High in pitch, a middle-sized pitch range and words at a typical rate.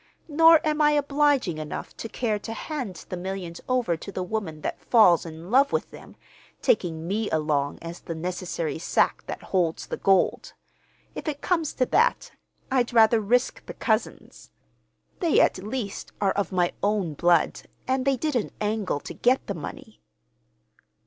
No: high, 210 Hz; wide, 7.0 semitones; average, 165 wpm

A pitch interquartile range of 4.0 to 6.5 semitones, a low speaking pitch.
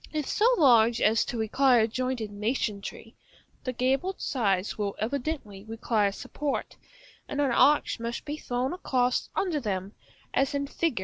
No: average, 4.4 semitones; high, 245 Hz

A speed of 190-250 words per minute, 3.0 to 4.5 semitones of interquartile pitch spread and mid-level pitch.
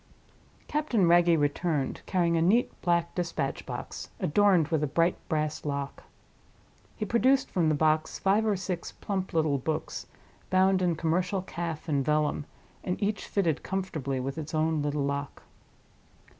No: average, 150 wpm; average, 3.8 semitones; medium, 165 Hz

